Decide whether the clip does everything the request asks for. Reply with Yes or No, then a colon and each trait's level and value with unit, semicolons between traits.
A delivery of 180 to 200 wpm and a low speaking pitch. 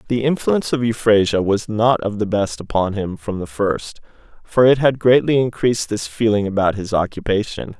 Yes: average, 185 wpm; low, 110 Hz